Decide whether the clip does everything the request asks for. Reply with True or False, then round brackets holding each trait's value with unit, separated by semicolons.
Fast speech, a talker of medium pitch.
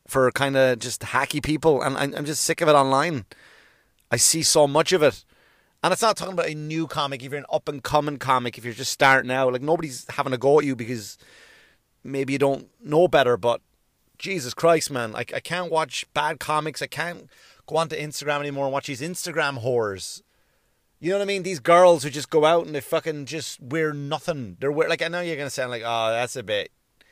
True (230 wpm; 150 Hz)